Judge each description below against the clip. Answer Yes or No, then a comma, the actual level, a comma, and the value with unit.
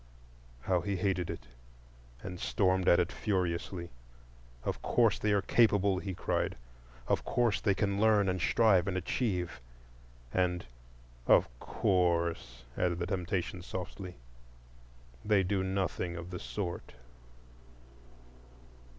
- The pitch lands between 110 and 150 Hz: No, very low, 95 Hz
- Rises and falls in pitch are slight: Yes, narrow, 2.2 semitones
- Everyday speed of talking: No, slow, 120 wpm